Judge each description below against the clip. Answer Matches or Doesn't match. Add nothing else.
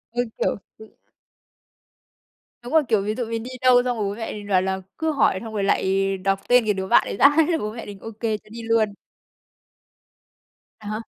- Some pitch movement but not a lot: Matches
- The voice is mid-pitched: Doesn't match